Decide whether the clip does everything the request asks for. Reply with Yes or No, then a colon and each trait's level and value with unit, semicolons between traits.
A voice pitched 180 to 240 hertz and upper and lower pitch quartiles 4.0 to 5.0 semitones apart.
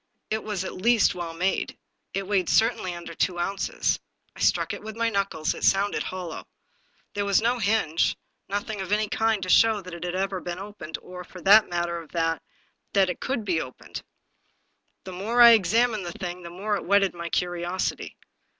No: high, 190 Hz; average, 3.4 semitones